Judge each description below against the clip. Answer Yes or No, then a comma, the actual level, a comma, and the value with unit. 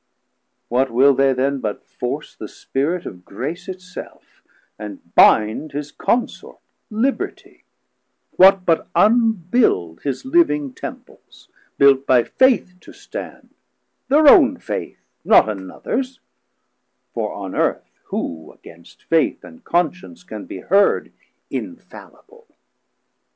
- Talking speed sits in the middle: No, slow, 115 wpm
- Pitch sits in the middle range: Yes, medium, 160 Hz